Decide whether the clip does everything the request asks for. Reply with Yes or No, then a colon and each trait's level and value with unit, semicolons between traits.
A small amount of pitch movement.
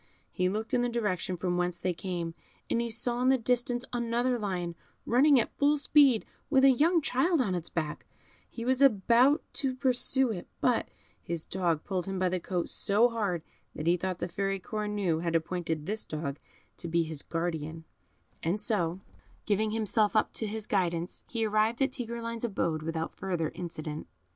No: wide, 5.6 semitones